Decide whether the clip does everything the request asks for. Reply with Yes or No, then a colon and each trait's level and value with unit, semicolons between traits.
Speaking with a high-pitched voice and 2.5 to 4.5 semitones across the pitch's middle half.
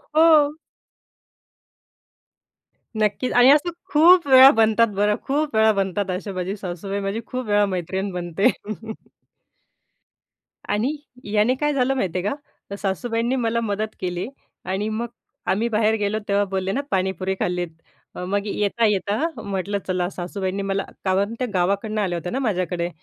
Yes: high, 205 Hz; average, 3.6 semitones